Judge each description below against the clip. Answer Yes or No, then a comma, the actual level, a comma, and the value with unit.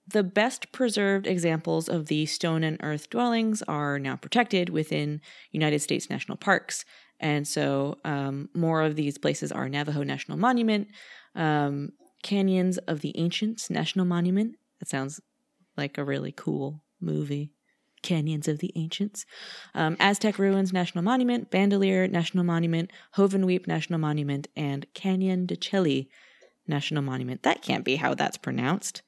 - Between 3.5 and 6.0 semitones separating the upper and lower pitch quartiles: Yes, average, 4.7 semitones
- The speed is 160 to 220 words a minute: No, average, 145 wpm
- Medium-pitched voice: Yes, medium, 170 Hz